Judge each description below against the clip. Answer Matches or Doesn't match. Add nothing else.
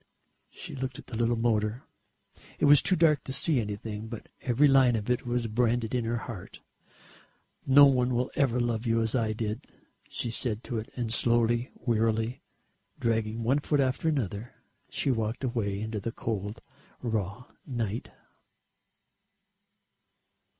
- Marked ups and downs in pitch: Doesn't match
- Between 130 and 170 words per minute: Matches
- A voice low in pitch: Matches